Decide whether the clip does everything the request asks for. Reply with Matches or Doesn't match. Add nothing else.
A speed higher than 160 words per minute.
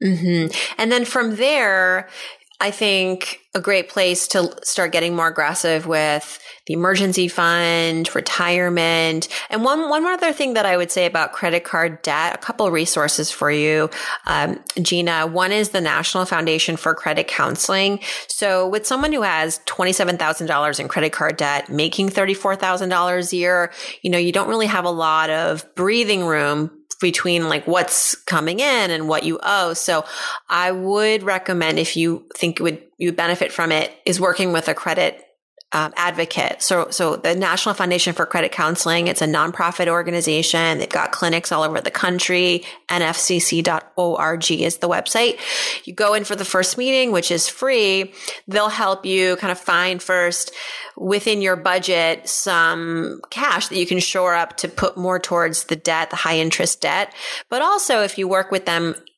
Matches